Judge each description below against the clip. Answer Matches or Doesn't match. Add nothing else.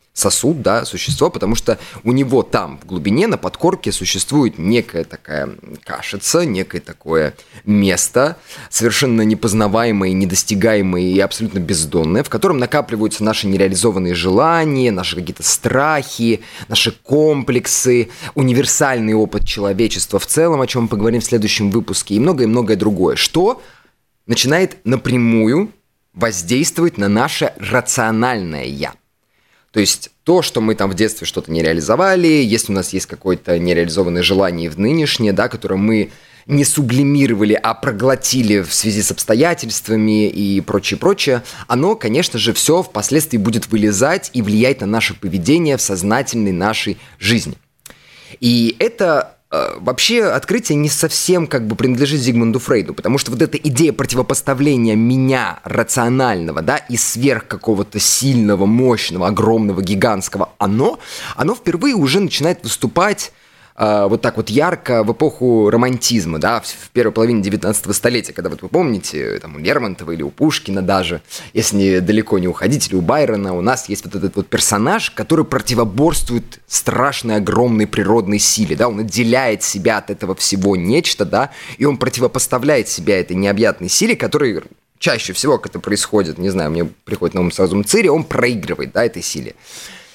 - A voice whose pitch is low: Matches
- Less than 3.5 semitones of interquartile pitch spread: Doesn't match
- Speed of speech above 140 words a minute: Matches